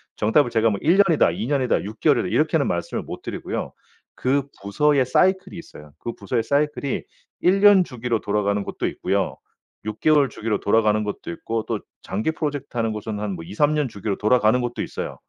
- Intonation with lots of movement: Yes, wide, 5.7 semitones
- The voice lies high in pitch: No, low, 120 Hz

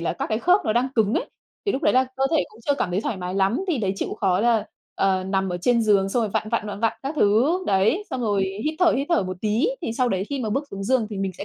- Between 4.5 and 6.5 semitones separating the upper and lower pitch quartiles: Yes, average, 4.8 semitones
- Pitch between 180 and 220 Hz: Yes, high, 215 Hz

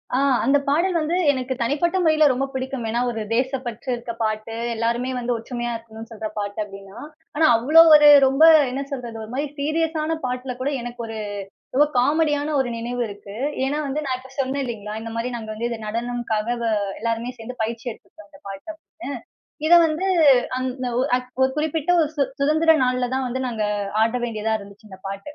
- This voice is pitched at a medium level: No, very high, 250 Hz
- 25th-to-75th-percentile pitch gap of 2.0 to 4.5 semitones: Yes, average, 4.1 semitones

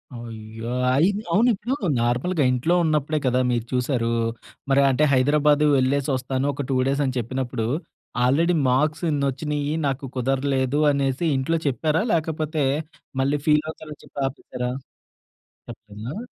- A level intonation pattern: No, average, 3.1 semitones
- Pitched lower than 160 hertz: Yes, medium, 140 Hz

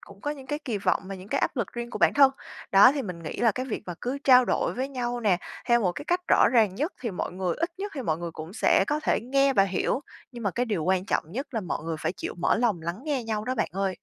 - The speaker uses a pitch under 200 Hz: No, high, 230 Hz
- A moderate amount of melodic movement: No, wide, 5.7 semitones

